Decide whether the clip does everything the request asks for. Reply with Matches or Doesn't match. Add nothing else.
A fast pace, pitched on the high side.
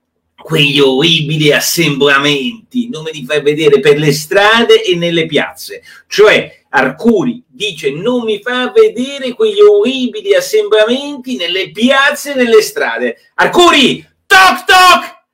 Doesn't match